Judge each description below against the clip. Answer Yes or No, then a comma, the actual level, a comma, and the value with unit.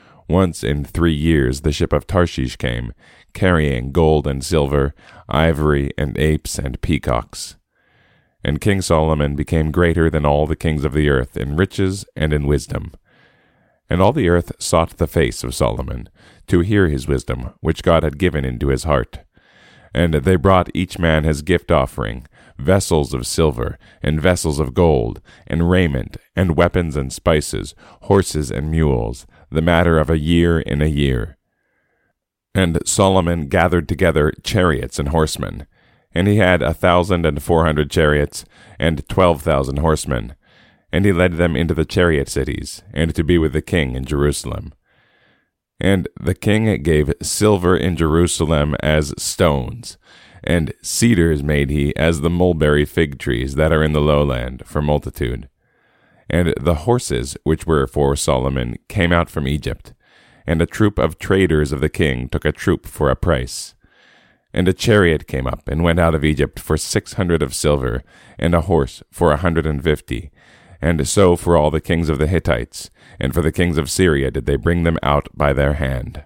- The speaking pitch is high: No, very low, 80 Hz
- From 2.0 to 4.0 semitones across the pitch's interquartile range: Yes, average, 3.1 semitones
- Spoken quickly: No, average, 170 wpm